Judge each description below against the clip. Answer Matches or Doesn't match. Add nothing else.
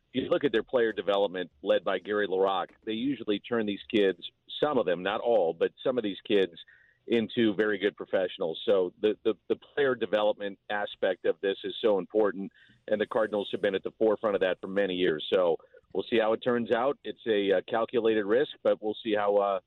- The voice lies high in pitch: Doesn't match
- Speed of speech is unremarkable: Doesn't match